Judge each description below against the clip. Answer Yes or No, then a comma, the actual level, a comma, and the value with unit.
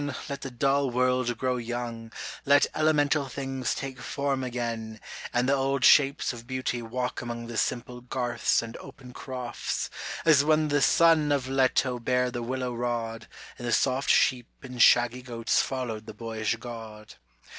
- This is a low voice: Yes, low, 125 Hz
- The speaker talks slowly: No, average, 160 wpm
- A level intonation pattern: Yes, narrow, 2.3 semitones